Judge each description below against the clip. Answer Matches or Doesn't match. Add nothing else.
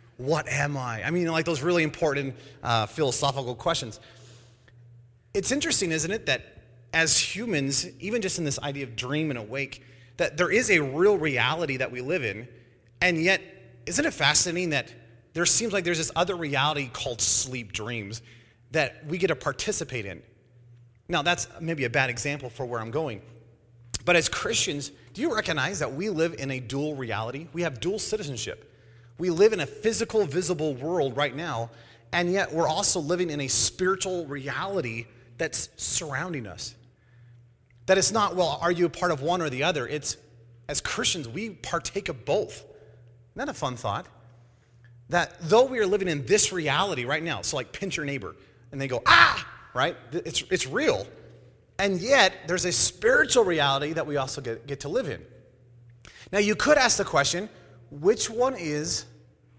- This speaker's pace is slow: Doesn't match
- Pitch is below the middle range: Doesn't match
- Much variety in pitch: Matches